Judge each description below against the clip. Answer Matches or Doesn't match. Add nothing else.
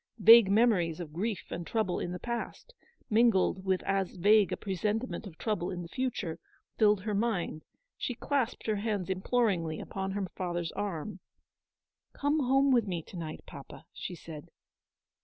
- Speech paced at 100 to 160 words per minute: Doesn't match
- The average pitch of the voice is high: Matches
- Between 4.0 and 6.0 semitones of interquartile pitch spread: Matches